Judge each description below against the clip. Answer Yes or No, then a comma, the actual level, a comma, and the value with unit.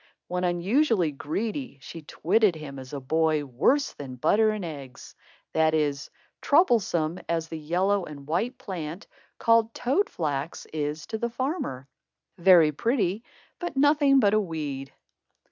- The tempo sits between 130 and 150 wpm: Yes, average, 145 wpm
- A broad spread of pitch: Yes, wide, 6.8 semitones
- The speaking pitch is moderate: Yes, medium, 170 Hz